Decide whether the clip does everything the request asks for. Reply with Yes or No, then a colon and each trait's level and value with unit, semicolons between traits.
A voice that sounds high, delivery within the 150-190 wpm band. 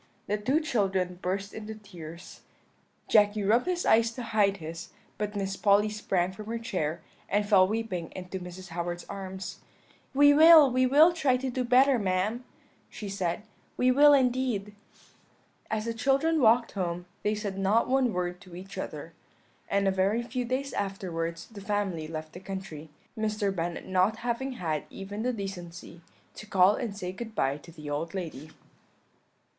Yes: high, 200 Hz; average, 170 wpm